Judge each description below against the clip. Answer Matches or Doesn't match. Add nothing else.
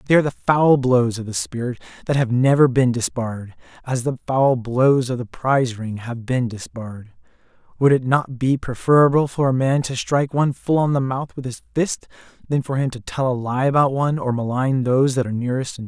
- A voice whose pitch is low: Matches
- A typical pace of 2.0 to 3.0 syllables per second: Matches